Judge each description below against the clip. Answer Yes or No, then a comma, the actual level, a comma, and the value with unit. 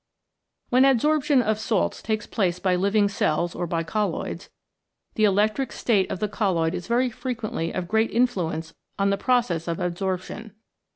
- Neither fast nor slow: Yes, average, 160 wpm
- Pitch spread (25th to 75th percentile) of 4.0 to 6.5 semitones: Yes, average, 4.4 semitones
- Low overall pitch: No, high, 205 Hz